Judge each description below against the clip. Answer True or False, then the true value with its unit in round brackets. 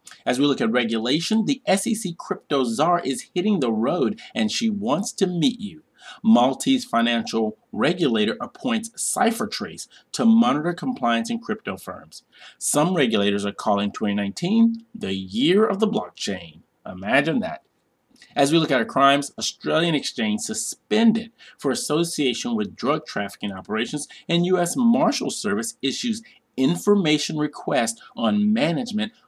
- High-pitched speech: True (205 Hz)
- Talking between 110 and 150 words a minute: True (135 wpm)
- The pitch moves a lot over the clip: True (8.6 semitones)